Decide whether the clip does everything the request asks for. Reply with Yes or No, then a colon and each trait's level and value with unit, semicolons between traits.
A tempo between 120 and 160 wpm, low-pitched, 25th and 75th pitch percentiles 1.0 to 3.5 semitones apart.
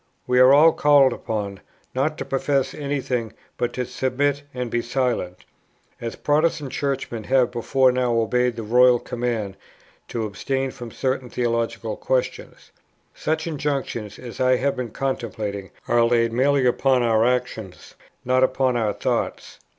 Yes: average, 145 wpm; low, 125 Hz; narrow, 2.5 semitones